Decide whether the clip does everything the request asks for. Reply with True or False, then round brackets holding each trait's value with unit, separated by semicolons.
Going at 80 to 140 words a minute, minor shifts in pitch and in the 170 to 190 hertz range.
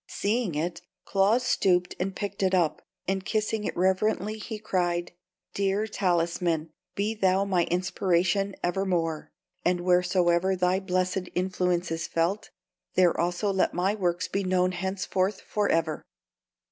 True (135 wpm; 2.0 semitones; 185 Hz)